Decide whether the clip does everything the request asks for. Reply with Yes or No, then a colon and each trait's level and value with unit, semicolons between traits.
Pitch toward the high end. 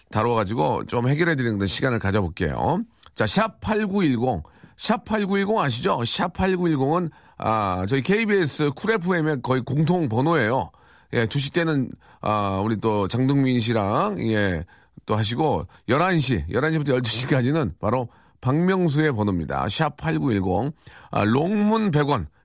No: low, 135 Hz